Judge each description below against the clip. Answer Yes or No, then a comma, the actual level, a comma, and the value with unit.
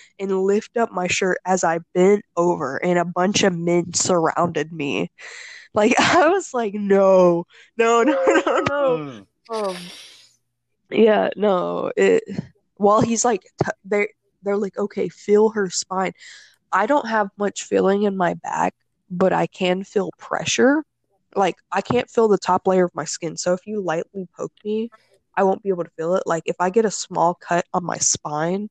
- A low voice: No, high, 195 Hz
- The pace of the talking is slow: No, average, 180 wpm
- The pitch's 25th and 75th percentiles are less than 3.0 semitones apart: No, average, 3.6 semitones